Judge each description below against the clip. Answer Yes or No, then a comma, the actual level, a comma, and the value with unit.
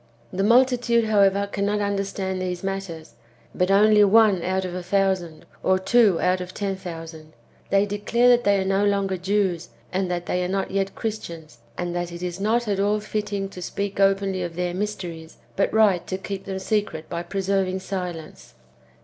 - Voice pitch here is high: Yes, high, 195 Hz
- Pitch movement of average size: No, narrow, 2.1 semitones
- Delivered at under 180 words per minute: No, average, 185 wpm